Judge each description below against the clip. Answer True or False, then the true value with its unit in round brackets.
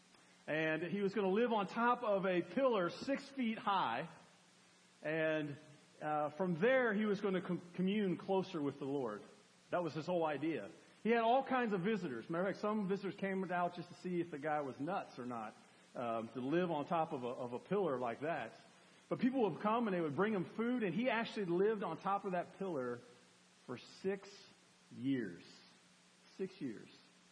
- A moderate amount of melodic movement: True (4.8 semitones)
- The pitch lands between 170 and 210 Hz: True (185 Hz)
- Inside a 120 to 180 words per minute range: False (200 wpm)